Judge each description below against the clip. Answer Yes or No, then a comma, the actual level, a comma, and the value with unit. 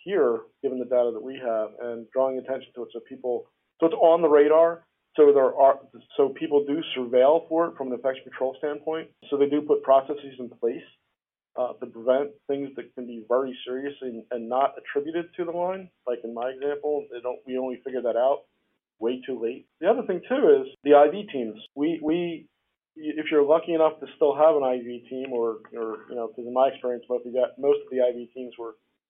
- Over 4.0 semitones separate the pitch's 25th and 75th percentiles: Yes, average, 4.4 semitones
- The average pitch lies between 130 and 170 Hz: Yes, low, 135 Hz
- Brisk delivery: Yes, fast, 215 wpm